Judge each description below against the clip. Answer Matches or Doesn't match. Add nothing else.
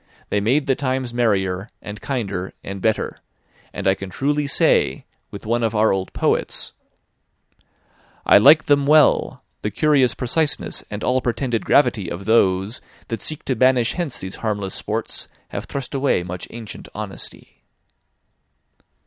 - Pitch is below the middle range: Matches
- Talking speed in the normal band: Matches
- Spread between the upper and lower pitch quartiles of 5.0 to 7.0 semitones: Matches